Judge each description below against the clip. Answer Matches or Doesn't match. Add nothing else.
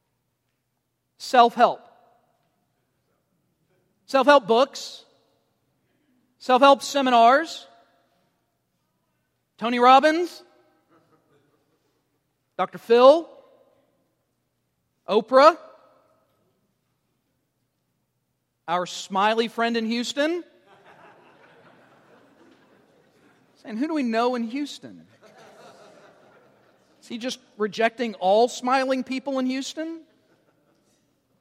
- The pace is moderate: Doesn't match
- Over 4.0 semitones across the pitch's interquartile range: Matches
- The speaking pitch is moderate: Doesn't match